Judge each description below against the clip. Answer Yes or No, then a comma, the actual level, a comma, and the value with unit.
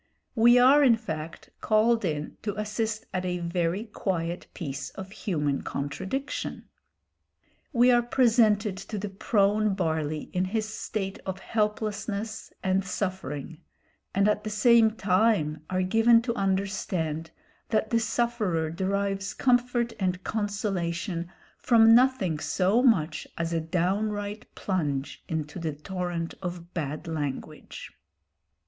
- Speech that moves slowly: Yes, slow, 125 wpm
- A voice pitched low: No, high, 195 Hz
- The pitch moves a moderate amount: Yes, average, 4.6 semitones